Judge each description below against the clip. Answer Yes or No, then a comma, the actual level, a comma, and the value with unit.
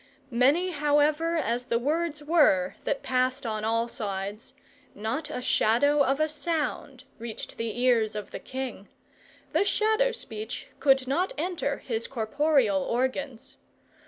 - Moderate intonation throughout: Yes, average, 4.8 semitones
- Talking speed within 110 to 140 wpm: Yes, slow, 135 wpm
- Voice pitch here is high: Yes, very high, 265 Hz